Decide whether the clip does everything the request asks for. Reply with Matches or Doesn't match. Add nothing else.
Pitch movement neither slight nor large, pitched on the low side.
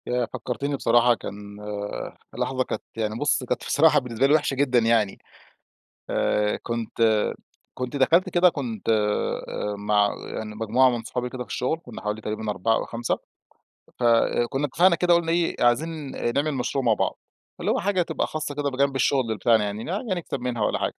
Matches